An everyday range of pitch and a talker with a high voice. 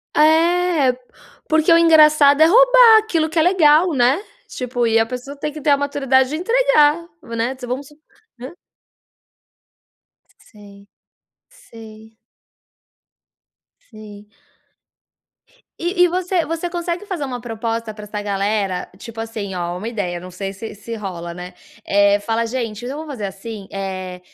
No: wide, 7.3 semitones; very high, 250 Hz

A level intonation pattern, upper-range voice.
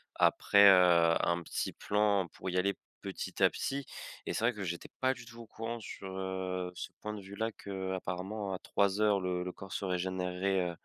No: narrow, 2.3 semitones; very low, 95 Hz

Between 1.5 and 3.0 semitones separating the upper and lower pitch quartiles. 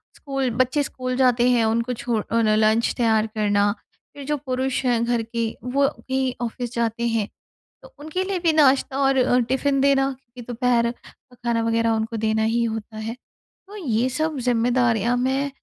Yes: average, 2.7 semitones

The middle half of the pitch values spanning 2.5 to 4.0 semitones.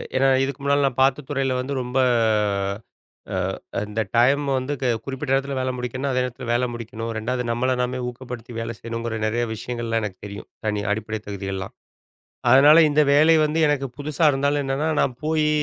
Yes: average, 3.1 semitones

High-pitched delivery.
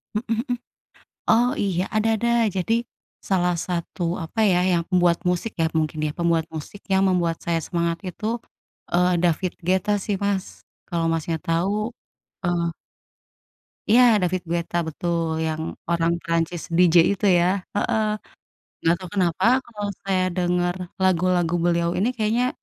No: medium, 175 Hz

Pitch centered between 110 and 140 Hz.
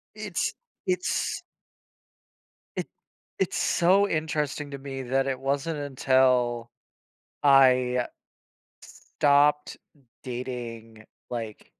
Yes: low, 135 Hz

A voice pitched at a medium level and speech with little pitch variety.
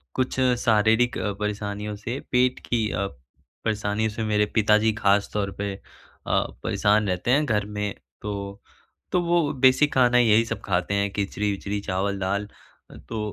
No: low, 105 Hz; narrow, 2.3 semitones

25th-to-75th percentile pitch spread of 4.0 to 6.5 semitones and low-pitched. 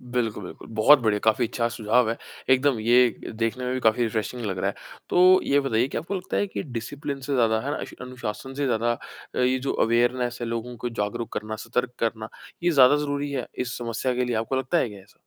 No: average, 2.7 semitones; low, 120 Hz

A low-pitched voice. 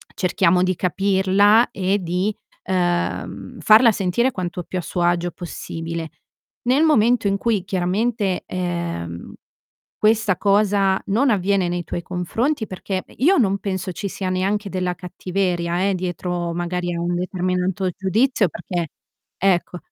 No: medium, 185 Hz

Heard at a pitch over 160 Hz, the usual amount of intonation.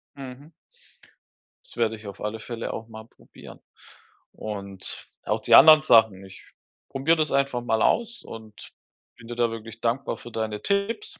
No: low, 115 Hz; average, 4.0 semitones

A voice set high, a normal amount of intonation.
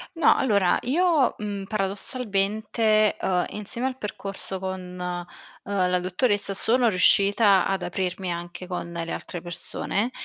Yes: high, 195 Hz; average, 3.0 semitones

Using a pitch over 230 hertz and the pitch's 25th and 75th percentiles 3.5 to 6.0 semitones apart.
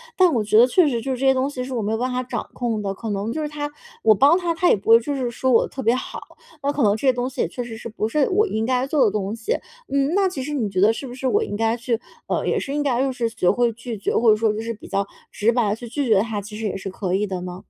Yes: high, 240 Hz; average, 3.9 semitones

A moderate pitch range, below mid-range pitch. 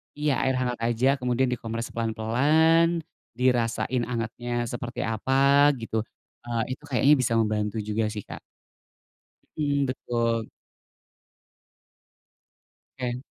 Yes: average, 3.0 semitones; low, 120 Hz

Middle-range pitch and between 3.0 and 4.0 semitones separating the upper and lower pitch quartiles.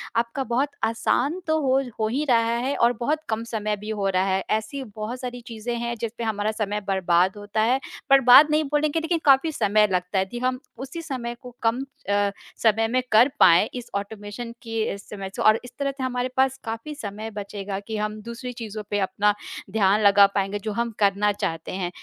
No: high, 225 Hz; average, 3.5 semitones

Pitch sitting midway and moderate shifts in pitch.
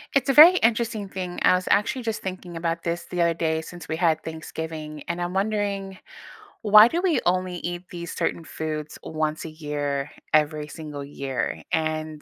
Yes: medium, 170 Hz; average, 3.6 semitones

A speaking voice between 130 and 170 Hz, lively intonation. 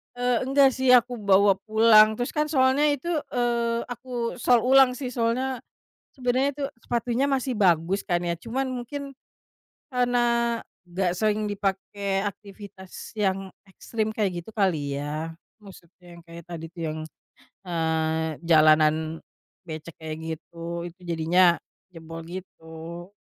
No: high, 200 Hz; wide, 6.4 semitones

